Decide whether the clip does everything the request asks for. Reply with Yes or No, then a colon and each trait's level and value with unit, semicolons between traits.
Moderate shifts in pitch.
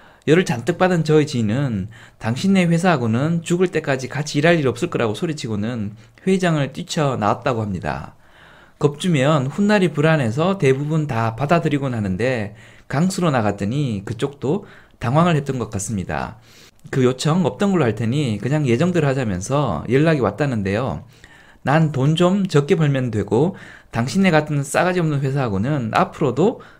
No: wide, 6.3 semitones